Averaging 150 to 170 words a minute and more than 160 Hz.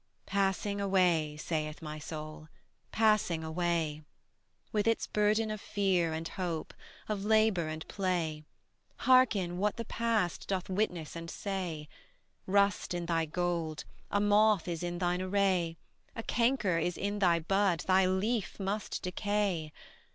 No: slow, 135 wpm; medium, 185 Hz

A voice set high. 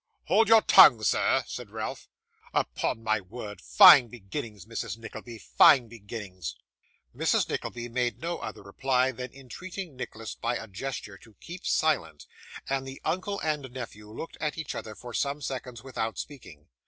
No: low, 120 Hz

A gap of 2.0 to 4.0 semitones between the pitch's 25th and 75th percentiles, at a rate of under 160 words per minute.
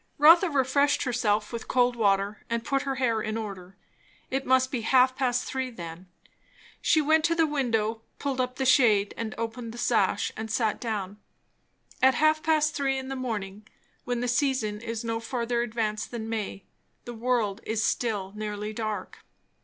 No: average, 3.5 semitones; average, 175 wpm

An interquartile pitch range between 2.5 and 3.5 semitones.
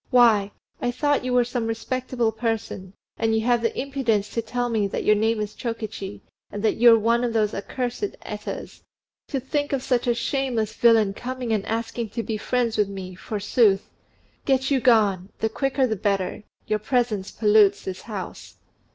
Yes: average, 2.9 semitones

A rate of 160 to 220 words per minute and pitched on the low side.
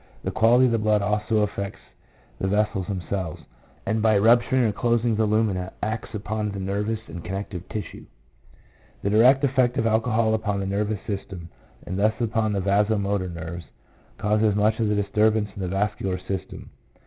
Yes: average, 170 wpm; low, 105 Hz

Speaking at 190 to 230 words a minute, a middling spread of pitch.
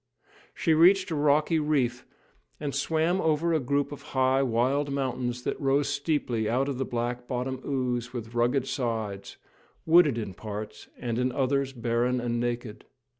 No: average, 160 wpm; average, 3.0 semitones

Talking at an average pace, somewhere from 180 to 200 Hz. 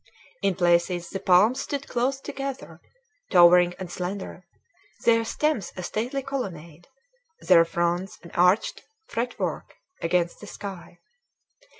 No: slow, 115 wpm; medium, 185 Hz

